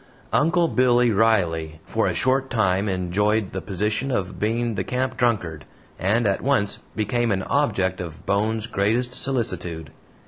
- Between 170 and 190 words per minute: No, average, 145 wpm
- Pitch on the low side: Yes, low, 105 Hz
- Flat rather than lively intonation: No, average, 4.5 semitones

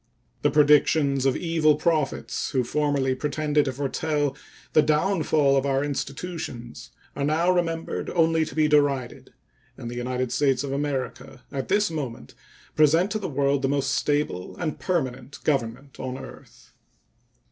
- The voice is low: No, medium, 145 Hz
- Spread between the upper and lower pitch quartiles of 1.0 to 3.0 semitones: Yes, narrow, 2.6 semitones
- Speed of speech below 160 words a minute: Yes, average, 145 wpm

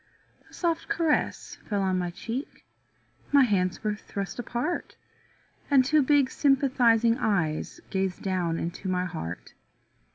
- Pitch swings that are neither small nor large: No, wide, 6.8 semitones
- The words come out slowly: Yes, slow, 130 wpm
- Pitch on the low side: No, high, 215 Hz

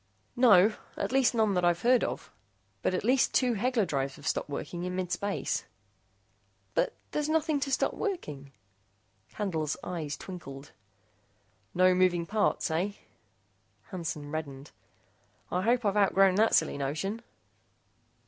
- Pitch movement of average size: No, wide, 6.0 semitones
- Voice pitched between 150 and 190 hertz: Yes, medium, 185 Hz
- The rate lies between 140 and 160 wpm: Yes, average, 145 wpm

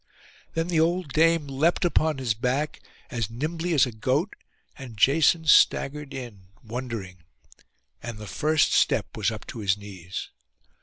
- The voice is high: No, low, 135 Hz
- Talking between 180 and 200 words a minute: No, average, 150 wpm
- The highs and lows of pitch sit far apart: Yes, wide, 6.0 semitones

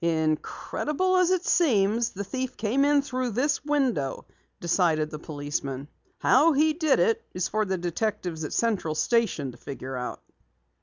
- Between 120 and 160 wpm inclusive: Yes, average, 150 wpm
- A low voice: No, high, 210 Hz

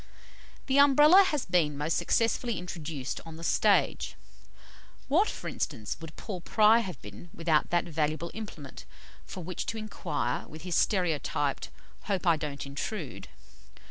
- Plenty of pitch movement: Yes, wide, 6.1 semitones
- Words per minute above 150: No, average, 145 wpm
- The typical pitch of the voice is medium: Yes, medium, 170 Hz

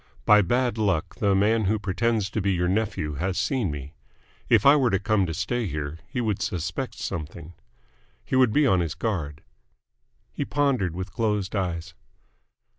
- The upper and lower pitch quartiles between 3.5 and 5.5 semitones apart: Yes, average, 4.5 semitones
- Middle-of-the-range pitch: No, low, 100 Hz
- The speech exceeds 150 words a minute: Yes, average, 175 wpm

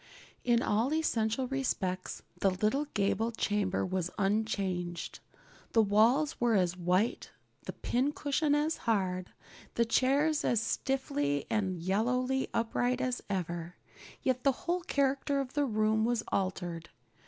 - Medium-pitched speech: No, high, 225 Hz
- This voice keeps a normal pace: No, slow, 130 wpm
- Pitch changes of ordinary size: No, wide, 5.8 semitones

